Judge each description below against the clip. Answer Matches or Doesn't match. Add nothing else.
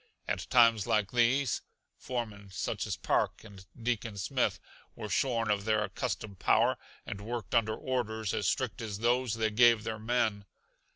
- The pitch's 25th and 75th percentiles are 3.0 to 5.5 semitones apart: Doesn't match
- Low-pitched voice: Matches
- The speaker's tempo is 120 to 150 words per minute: Doesn't match